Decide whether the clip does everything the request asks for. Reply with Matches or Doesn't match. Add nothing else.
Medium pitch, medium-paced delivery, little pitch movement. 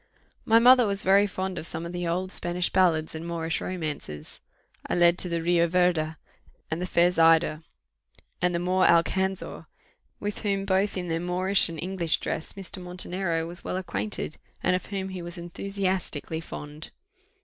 Matches